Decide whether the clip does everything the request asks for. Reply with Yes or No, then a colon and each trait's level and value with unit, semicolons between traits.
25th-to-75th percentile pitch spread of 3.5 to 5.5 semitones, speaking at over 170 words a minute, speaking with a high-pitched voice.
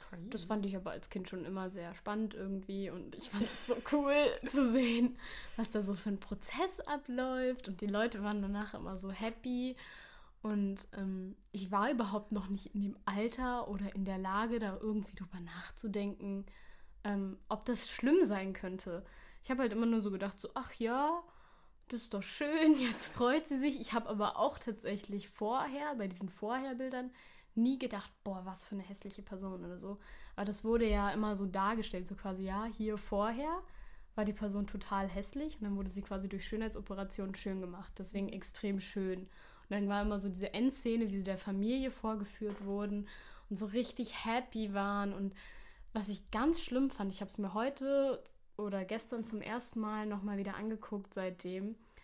No: average, 3.0 semitones; average, 185 wpm; high, 205 Hz